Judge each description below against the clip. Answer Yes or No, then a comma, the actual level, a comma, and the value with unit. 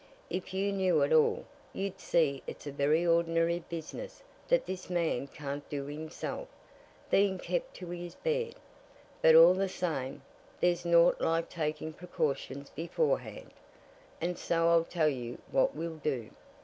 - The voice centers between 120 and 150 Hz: No, medium, 170 Hz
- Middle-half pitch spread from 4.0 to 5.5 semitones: No, average, 3.3 semitones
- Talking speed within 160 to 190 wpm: No, average, 150 wpm